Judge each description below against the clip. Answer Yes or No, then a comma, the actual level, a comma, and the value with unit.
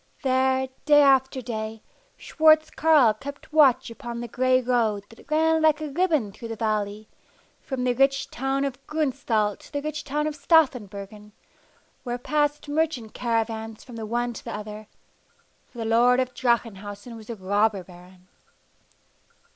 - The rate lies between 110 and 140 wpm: No, average, 155 wpm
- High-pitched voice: Yes, high, 245 Hz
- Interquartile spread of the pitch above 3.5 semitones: Yes, average, 4.6 semitones